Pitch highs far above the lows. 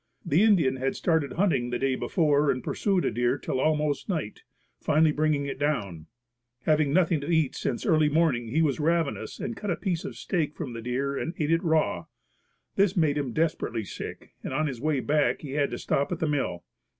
No: average, 3.3 semitones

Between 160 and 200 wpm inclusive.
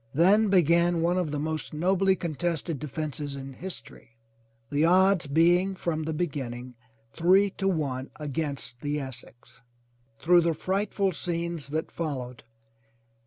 No: slow, 135 wpm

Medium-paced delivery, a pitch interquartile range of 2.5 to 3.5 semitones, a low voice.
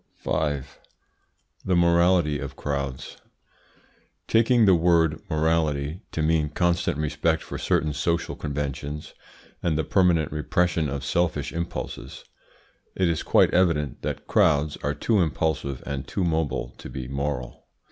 No: slow, 130 wpm; average, 2.9 semitones; very low, 80 Hz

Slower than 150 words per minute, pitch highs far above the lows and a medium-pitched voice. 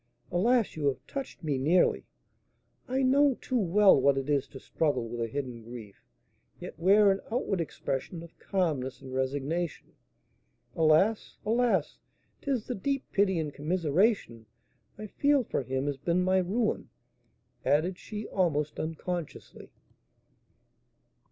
Yes: slow, 135 wpm; wide, 6.8 semitones; medium, 170 Hz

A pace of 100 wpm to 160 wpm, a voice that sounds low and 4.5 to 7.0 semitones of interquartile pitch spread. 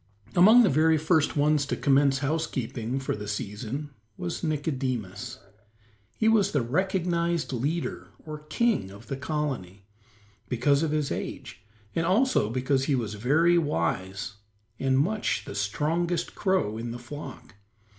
No: average, 140 wpm; medium, 145 Hz; wide, 5.6 semitones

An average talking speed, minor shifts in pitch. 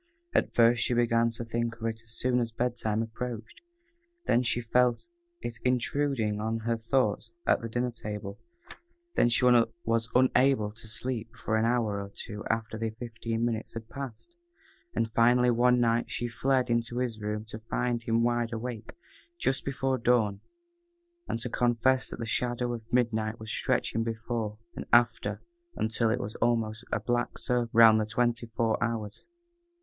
Yes: average, 170 wpm; narrow, 1.6 semitones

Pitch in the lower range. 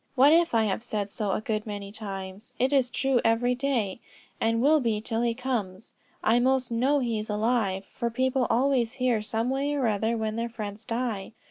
No: high, 230 Hz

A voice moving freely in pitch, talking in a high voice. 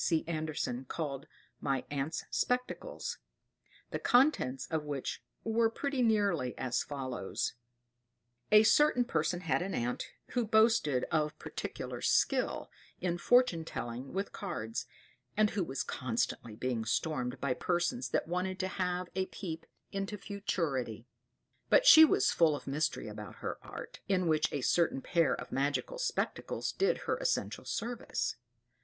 No: wide, 7.4 semitones; medium, 165 Hz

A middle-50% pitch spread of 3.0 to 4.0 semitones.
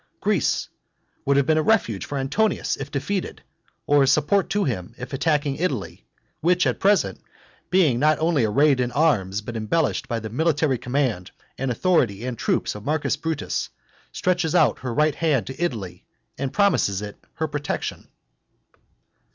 No: average, 5.2 semitones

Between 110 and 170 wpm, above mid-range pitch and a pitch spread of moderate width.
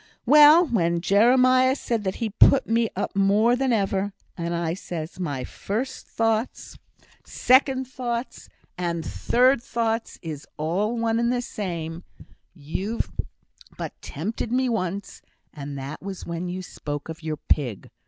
No: average, 145 wpm; high, 200 Hz; wide, 6.0 semitones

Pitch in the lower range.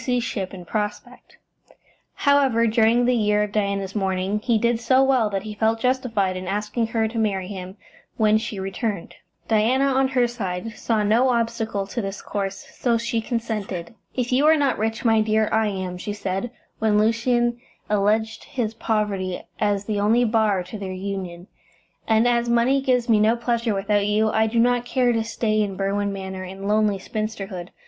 No: high, 215 Hz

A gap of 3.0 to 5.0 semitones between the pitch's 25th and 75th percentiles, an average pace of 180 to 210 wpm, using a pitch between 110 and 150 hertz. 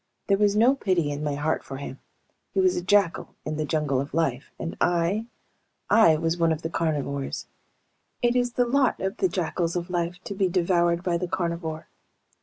No: average, 4.1 semitones; average, 200 wpm; medium, 170 Hz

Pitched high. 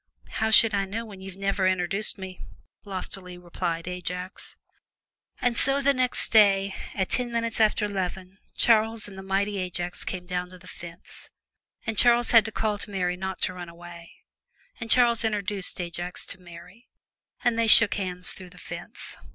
Yes: high, 195 Hz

